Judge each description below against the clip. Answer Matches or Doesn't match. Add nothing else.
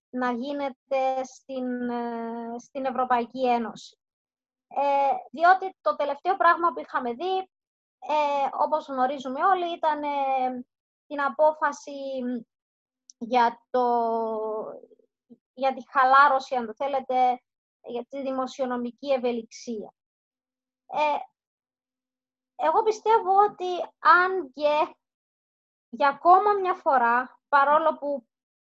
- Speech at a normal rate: Doesn't match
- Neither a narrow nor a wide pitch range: Matches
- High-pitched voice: Matches